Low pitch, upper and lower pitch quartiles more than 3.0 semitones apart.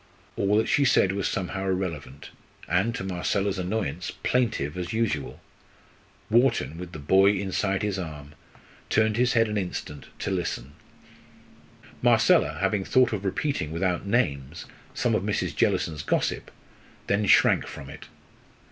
Yes: very low, 95 Hz; average, 4.4 semitones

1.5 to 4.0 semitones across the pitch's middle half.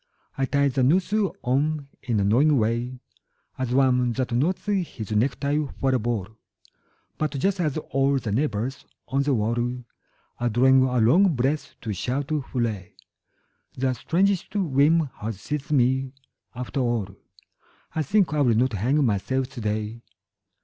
Yes: average, 3.5 semitones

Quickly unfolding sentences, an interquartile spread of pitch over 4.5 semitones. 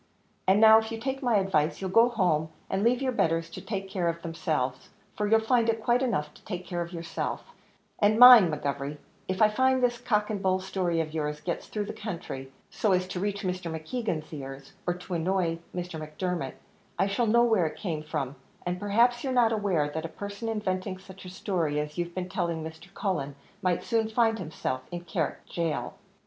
Yes: fast, 210 wpm; average, 5.0 semitones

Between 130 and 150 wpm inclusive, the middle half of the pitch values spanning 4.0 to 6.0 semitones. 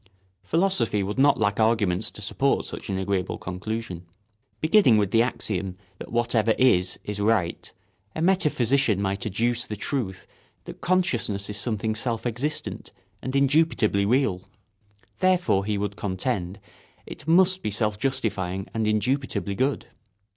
Yes: average, 140 wpm; average, 4.9 semitones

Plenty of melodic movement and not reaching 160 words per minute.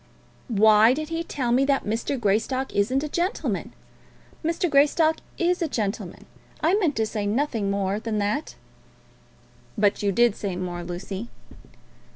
Yes: wide, 6.6 semitones; average, 150 wpm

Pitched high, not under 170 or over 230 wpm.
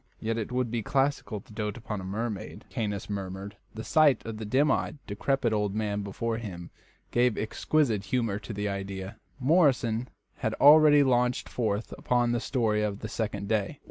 No: low, 110 Hz; average, 175 wpm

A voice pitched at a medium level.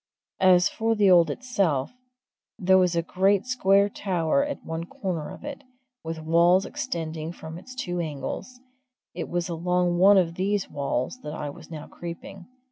Yes: medium, 180 Hz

